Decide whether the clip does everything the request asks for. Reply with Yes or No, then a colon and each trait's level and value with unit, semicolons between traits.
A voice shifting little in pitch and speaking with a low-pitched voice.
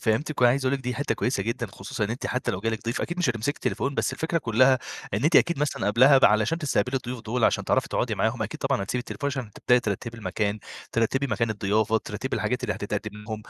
No: average, 3.7 semitones; low, 120 Hz